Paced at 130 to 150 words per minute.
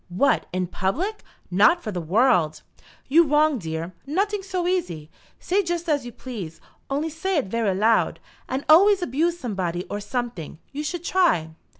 No: average, 165 wpm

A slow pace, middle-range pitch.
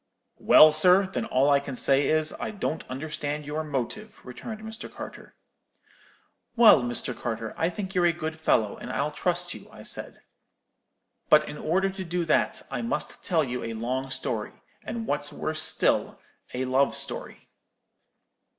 No: average, 160 wpm; medium, 155 Hz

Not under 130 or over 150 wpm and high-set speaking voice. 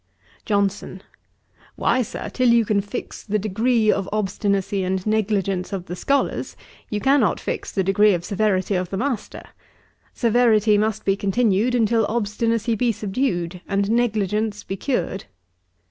Yes: average, 145 wpm; high, 210 Hz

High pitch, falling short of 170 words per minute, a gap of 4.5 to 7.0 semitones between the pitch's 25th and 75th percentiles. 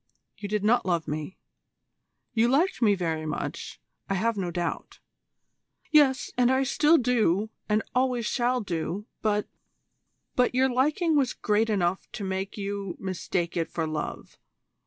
Yes: high, 210 Hz; average, 160 wpm; wide, 5.5 semitones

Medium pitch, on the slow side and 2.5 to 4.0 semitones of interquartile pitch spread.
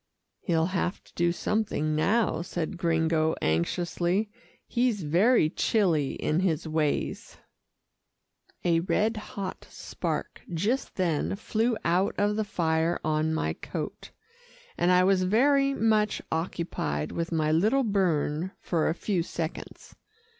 No: medium, 175 Hz; slow, 125 wpm; average, 4.5 semitones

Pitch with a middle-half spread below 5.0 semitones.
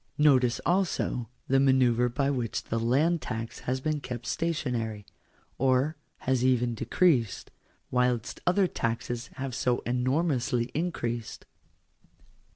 Yes: average, 3.2 semitones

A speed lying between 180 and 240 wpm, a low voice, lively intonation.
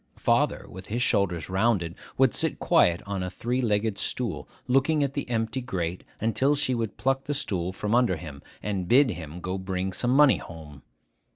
Yes: average, 185 wpm; low, 105 Hz; wide, 5.8 semitones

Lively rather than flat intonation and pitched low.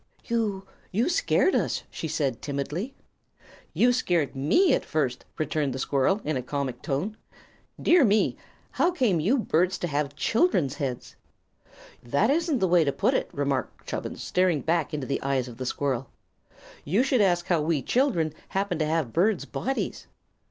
No: wide, 7.4 semitones; medium, 165 Hz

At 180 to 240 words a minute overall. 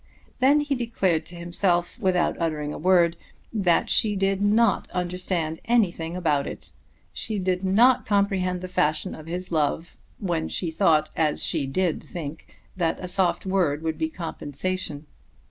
No: average, 155 wpm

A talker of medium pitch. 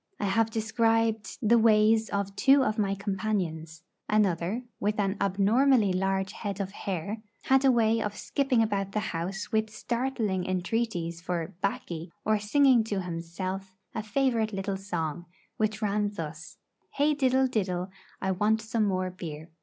No: high, 205 Hz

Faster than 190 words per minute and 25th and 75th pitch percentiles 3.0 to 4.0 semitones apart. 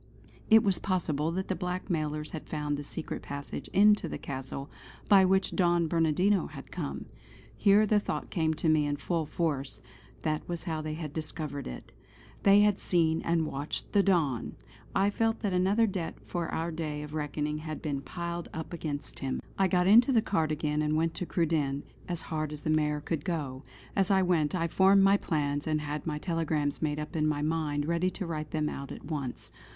Yes: average, 200 wpm; average, 3.3 semitones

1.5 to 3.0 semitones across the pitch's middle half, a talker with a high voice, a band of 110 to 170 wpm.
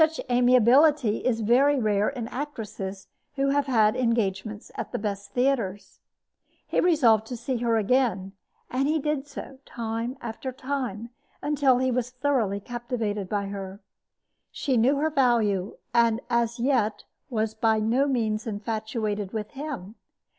No: average, 3.7 semitones; high, 235 Hz; average, 145 wpm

